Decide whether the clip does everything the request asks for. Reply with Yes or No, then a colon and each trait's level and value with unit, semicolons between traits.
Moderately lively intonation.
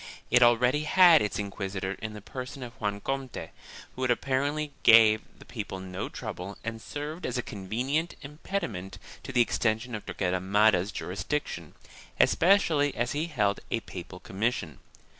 No: wide, 5.7 semitones